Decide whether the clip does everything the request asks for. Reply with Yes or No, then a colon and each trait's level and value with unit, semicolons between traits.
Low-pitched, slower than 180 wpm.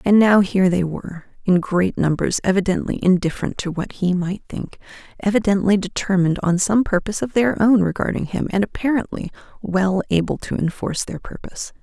No: high, 190 Hz; average, 165 wpm